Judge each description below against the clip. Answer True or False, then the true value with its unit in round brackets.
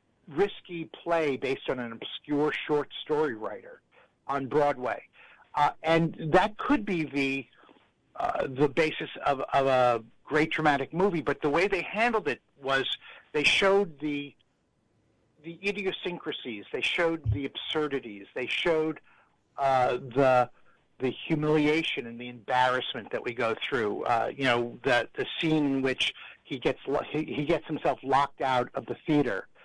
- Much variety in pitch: False (3.9 semitones)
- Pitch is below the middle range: False (145 Hz)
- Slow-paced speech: False (150 wpm)